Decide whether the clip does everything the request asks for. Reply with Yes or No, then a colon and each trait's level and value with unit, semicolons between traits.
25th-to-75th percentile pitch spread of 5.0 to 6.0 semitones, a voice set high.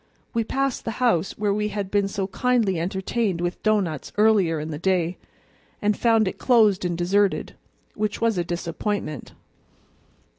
No: average, 3.7 semitones; high, 200 Hz